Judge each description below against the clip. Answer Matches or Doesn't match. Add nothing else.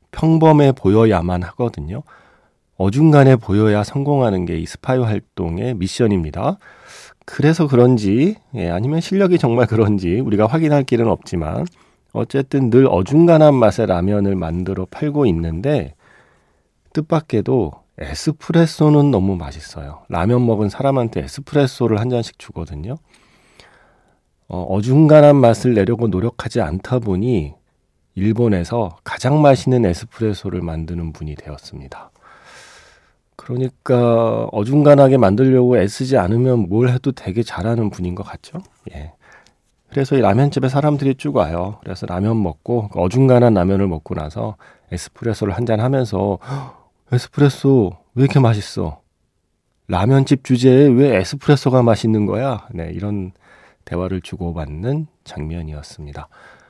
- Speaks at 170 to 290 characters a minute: Doesn't match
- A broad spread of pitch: Matches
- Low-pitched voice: Matches